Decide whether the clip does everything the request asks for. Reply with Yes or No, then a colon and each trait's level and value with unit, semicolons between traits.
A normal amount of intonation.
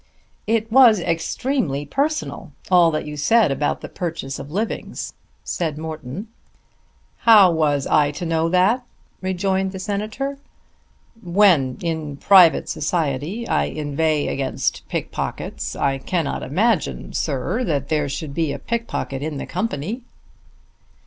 No: wide, 6.0 semitones